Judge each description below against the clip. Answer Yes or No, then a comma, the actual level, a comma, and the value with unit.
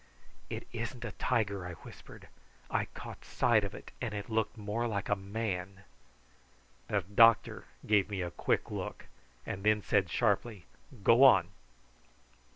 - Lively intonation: No, average, 2.8 semitones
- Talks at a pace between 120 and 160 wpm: Yes, average, 150 wpm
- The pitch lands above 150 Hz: No, low, 105 Hz